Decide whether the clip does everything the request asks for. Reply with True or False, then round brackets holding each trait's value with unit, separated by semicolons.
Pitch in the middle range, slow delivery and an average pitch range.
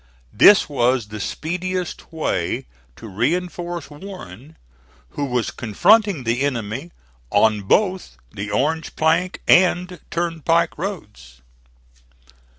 False (155 Hz; 100 wpm; 7.6 semitones)